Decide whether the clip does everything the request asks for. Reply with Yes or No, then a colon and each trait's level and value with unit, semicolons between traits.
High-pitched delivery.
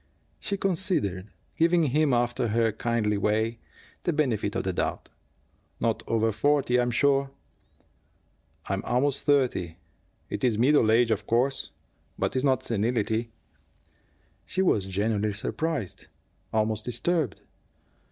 No: low, 120 Hz